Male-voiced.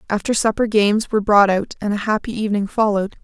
No: female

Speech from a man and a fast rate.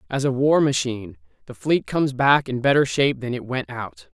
Yes: male; fast, 215 wpm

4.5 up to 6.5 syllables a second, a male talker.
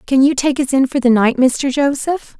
No: 4.9 syllables/s; female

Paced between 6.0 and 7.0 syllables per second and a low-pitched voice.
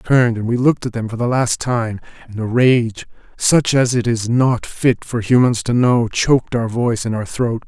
No: 5.4 syllables/s; low, 120 Hz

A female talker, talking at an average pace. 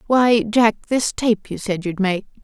Yes: female; average, 195 wpm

